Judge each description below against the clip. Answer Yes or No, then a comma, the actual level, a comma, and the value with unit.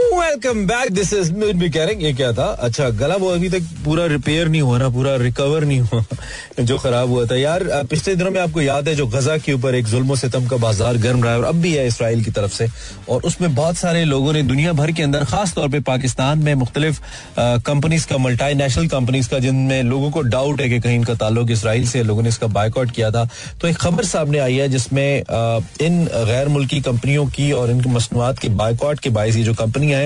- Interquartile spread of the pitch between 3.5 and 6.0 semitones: Yes, average, 4.1 semitones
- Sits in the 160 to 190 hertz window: No, low, 135 Hz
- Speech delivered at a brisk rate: Yes, fast, 215 wpm